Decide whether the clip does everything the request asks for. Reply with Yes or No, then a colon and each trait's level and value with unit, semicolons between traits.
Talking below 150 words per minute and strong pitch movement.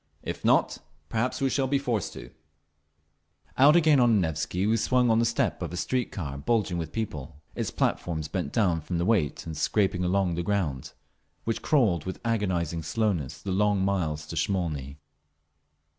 No: average, 175 wpm; wide, 5.7 semitones